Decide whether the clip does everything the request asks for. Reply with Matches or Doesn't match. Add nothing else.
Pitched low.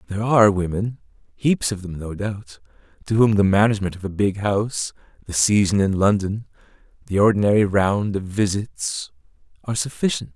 Matches